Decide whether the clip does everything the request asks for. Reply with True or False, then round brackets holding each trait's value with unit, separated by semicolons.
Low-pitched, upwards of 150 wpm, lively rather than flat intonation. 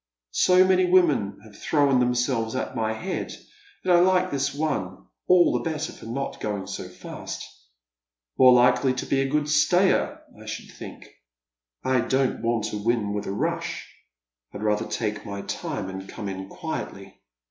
True (125 Hz; 170 wpm; 6.2 semitones)